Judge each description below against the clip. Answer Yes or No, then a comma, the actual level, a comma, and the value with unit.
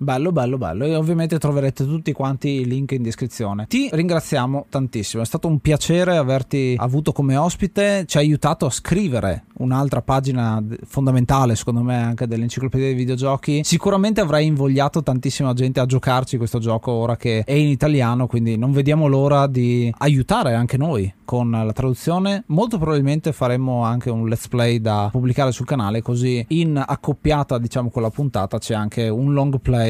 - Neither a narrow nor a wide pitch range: Yes, average, 3.5 semitones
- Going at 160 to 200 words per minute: Yes, fast, 170 wpm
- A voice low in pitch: Yes, low, 130 Hz